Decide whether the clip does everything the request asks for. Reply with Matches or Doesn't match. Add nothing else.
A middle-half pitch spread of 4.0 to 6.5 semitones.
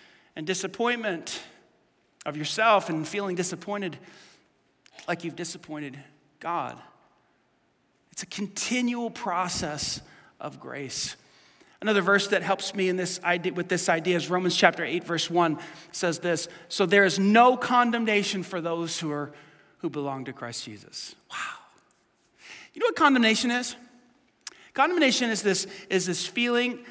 Matches